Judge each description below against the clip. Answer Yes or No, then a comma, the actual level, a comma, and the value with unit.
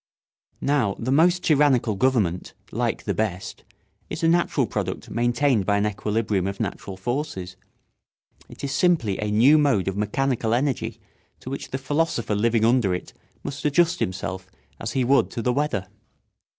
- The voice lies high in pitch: No, low, 120 Hz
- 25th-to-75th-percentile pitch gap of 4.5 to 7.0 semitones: Yes, wide, 5.5 semitones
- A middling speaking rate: Yes, average, 160 wpm